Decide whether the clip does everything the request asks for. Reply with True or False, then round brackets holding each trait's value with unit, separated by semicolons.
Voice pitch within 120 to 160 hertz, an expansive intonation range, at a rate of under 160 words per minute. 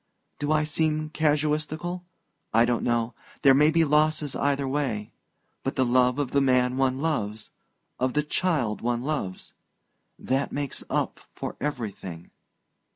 False (140 Hz; 3.7 semitones; 135 wpm)